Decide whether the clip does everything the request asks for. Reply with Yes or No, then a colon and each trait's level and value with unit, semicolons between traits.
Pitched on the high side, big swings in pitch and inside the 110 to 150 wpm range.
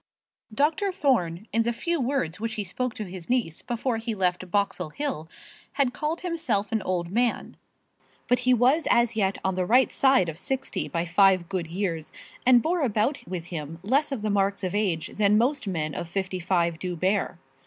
No: high, 205 Hz; wide, 5.8 semitones; average, 195 wpm